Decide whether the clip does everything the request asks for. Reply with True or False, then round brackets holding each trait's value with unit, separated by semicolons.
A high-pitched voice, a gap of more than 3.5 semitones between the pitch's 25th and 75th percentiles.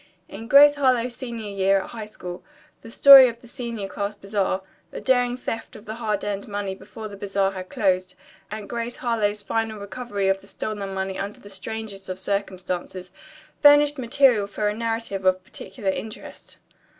False (210 Hz; 3.0 semitones)